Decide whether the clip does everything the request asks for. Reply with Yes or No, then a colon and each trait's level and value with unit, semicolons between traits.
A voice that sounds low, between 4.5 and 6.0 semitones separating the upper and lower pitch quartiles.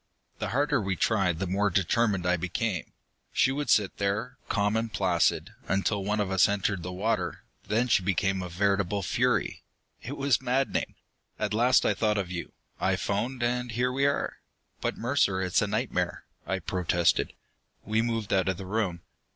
No: low, 100 Hz; average, 3.8 semitones